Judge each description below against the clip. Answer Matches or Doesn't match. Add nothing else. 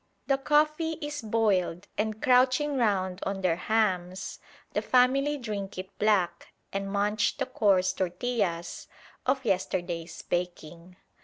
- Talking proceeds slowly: Matches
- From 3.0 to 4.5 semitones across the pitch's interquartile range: Doesn't match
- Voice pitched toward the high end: Matches